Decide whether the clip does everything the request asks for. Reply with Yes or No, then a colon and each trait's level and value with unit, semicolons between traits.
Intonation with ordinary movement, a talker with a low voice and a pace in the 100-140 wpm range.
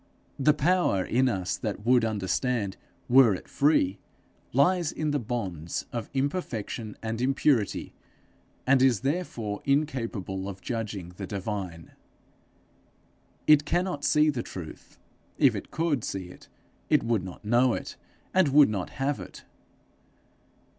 No: wide, 6.1 semitones; low, 120 Hz; slow, 135 wpm